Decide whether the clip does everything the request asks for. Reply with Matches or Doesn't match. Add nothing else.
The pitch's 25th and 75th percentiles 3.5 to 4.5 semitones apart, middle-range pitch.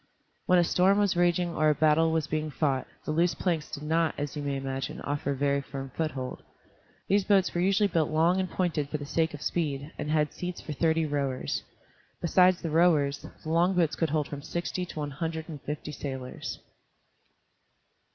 Doesn't match